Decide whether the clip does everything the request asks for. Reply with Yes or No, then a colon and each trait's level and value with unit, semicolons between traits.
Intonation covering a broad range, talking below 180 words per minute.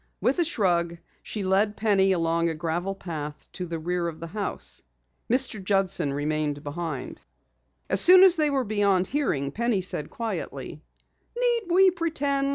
Yes: wide, 7.1 semitones; average, 160 wpm